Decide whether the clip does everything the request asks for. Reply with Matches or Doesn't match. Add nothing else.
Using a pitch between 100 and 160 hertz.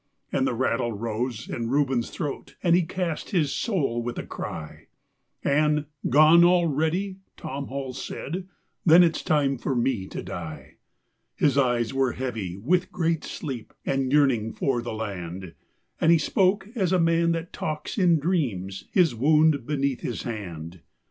Matches